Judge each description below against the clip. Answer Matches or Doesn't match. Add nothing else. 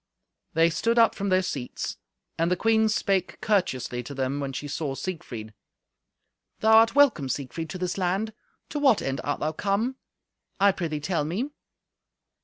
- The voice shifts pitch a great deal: Matches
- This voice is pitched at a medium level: Matches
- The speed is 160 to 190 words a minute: Matches